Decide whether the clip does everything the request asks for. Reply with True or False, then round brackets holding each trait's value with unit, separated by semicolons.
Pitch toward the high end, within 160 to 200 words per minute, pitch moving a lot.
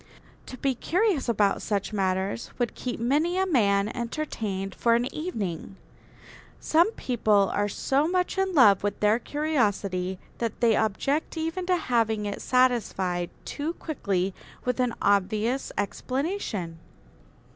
False (235 Hz; 135 wpm; 6.6 semitones)